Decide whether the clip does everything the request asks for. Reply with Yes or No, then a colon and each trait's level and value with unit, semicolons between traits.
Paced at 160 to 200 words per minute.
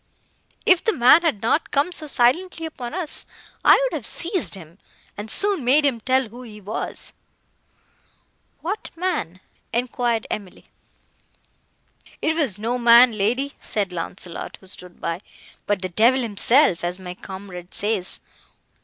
No: average, 145 wpm